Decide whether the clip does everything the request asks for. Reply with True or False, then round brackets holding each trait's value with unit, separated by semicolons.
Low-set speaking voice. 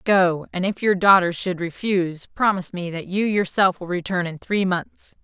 False (185 Hz)